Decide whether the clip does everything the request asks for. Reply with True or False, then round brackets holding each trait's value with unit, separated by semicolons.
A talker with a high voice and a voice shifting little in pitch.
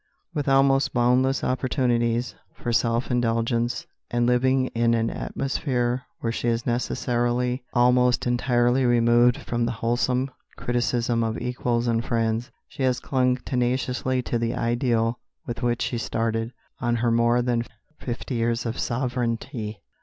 False (120 Hz; 1.2 semitones)